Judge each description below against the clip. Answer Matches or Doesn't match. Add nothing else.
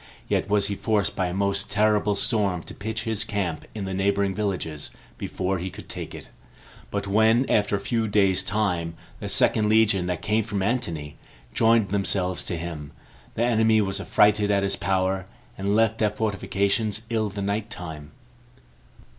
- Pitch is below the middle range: Matches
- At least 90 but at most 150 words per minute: Doesn't match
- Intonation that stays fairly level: Matches